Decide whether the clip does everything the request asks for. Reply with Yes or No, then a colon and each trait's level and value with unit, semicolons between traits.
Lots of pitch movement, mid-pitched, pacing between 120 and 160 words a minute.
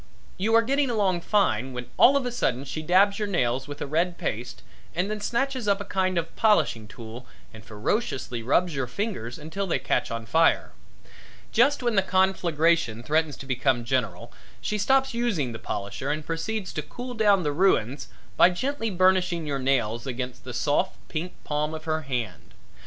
No: wide, 7.8 semitones; medium, 165 Hz; average, 185 wpm